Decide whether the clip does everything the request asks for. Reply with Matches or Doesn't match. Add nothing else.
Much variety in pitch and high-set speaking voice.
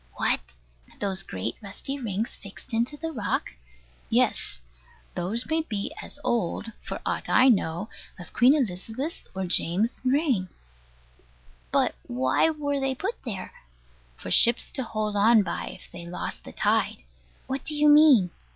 Matches